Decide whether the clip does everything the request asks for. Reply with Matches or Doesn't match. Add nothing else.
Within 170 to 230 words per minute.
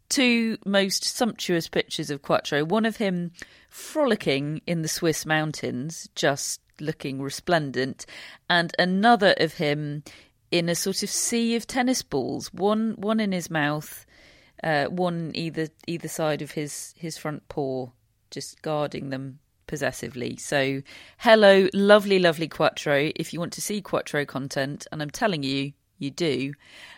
Doesn't match